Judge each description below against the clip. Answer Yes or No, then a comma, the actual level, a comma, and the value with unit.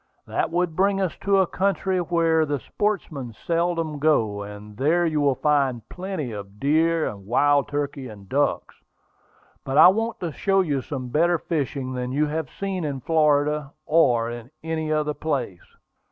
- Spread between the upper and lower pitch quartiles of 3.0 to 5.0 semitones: Yes, average, 4.4 semitones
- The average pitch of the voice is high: No, medium, 150 Hz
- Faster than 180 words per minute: No, average, 165 wpm